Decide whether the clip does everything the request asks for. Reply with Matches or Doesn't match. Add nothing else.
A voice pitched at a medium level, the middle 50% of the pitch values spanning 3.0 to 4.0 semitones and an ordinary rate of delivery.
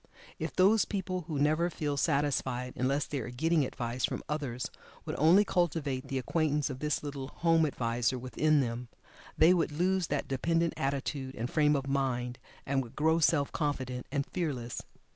Matches